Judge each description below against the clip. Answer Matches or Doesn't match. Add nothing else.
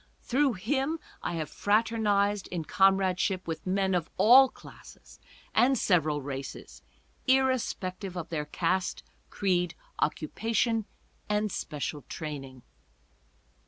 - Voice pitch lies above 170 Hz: Matches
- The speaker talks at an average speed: Doesn't match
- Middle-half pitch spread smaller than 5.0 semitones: Doesn't match